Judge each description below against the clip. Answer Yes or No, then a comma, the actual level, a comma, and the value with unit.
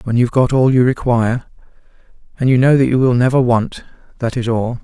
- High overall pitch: No, low, 125 Hz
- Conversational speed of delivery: No, fast, 210 wpm